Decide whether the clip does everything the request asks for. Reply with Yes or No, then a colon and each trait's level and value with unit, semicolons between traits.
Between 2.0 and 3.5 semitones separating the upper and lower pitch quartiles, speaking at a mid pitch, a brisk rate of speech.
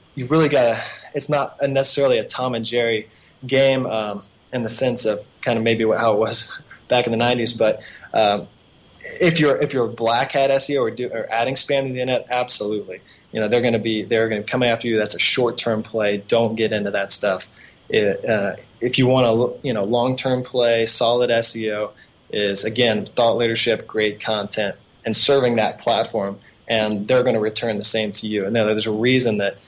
No: average, 2.8 semitones; low, 115 Hz; fast, 220 wpm